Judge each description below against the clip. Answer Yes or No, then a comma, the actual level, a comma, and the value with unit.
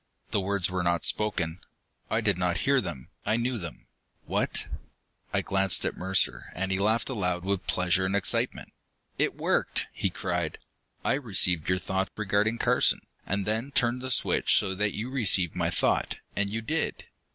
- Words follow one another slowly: No, average, 175 wpm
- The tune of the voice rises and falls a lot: No, average, 3.4 semitones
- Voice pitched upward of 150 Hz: No, low, 100 Hz